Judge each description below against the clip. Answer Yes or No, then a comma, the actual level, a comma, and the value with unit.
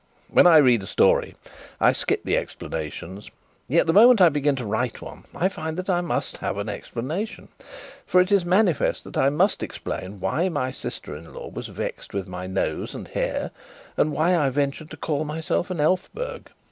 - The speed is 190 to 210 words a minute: Yes, average, 195 wpm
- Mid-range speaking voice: Yes, medium, 155 Hz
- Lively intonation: Yes, wide, 6.9 semitones